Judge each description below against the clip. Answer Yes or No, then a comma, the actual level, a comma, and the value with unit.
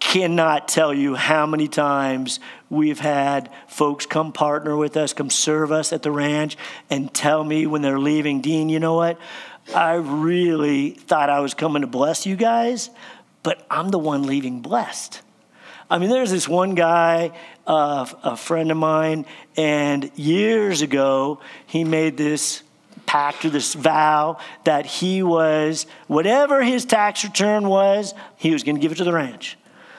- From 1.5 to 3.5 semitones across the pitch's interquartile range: Yes, narrow, 2.5 semitones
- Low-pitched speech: No, medium, 155 Hz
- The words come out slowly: No, average, 170 wpm